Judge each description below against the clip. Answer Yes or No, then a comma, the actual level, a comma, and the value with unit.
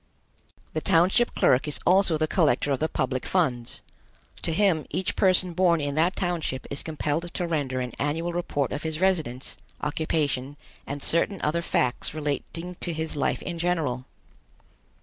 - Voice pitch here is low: No, medium, 160 Hz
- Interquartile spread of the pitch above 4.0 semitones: No, average, 3.5 semitones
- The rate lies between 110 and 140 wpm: No, average, 160 wpm